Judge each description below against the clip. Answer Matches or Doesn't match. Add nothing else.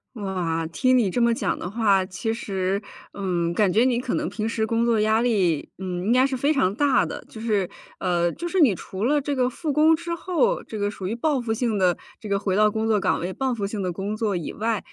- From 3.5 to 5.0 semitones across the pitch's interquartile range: Matches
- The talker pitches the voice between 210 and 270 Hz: Matches